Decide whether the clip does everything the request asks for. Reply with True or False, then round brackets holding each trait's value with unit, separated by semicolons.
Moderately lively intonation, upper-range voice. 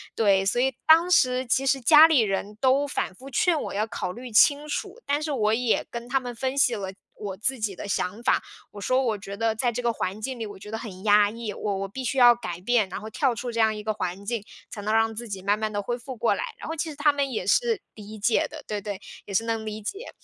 True (4.2 semitones; 230 Hz)